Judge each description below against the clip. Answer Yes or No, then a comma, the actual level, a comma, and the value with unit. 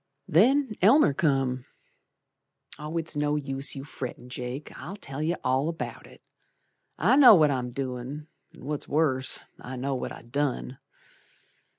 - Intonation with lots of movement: No, average, 3.5 semitones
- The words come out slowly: No, average, 145 wpm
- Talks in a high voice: No, medium, 140 Hz